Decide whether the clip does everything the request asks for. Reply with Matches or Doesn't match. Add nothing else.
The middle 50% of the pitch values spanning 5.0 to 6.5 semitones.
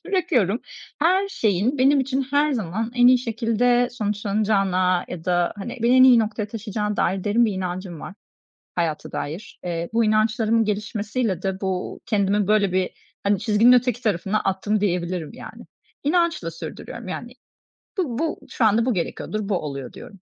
Doesn't match